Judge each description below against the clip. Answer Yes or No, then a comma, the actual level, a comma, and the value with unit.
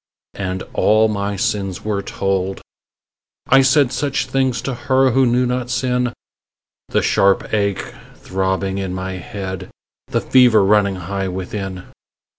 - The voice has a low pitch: Yes, low, 100 Hz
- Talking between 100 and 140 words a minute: Yes, slow, 135 wpm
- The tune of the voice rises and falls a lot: No, average, 4.7 semitones